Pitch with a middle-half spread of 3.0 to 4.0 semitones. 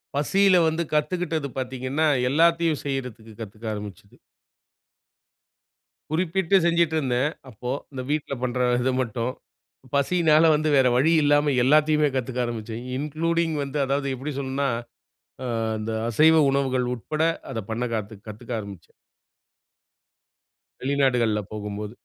No: average, 4.4 semitones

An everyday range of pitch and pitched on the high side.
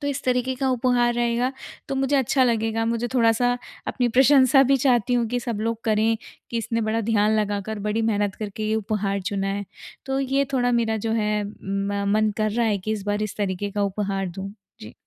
Yes: average, 3.0 semitones; high, 225 Hz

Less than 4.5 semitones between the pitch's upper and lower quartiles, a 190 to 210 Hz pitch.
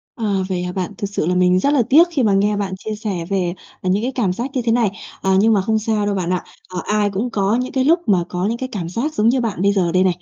Yes: average, 3.8 semitones; high, 205 Hz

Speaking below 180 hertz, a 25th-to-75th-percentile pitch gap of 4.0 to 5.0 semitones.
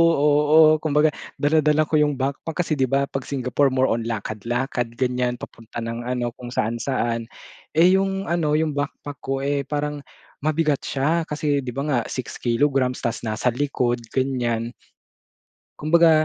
No: medium, 140 Hz; average, 3.6 semitones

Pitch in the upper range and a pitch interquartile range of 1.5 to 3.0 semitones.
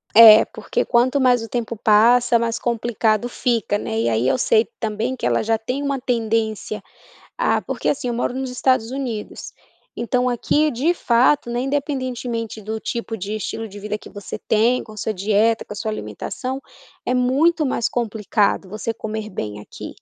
Yes: high, 230 Hz; average, 2.7 semitones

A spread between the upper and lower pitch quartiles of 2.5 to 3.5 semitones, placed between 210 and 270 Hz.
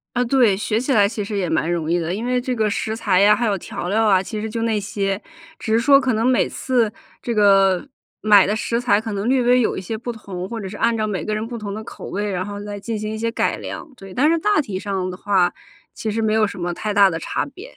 Yes: average, 2.9 semitones; high, 215 Hz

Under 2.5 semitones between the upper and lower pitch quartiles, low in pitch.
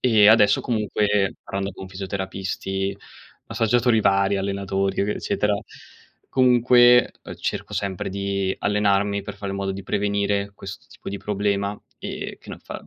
Yes: narrow, 1.2 semitones; low, 100 Hz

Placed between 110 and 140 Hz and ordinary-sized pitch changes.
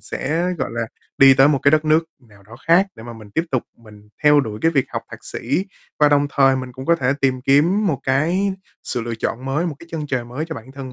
Yes: low, 135 Hz; average, 4.3 semitones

